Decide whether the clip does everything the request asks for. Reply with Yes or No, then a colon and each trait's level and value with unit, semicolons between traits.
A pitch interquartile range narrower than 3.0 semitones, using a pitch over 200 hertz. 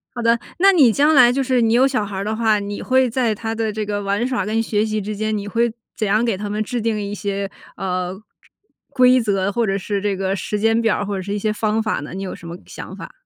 Yes: narrow, 2.6 semitones; high, 215 Hz